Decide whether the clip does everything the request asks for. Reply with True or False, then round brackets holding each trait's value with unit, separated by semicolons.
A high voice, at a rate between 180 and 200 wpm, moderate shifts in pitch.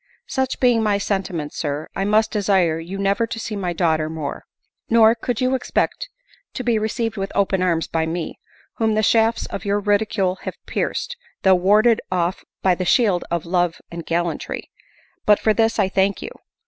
True (200 Hz; 185 wpm; 4.0 semitones)